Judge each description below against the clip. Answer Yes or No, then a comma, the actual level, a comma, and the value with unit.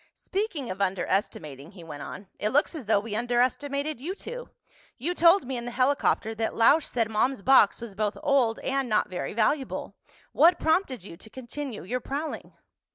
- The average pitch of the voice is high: Yes, high, 245 Hz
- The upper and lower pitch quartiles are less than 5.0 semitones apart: No, average, 5.3 semitones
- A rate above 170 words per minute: Yes, average, 180 wpm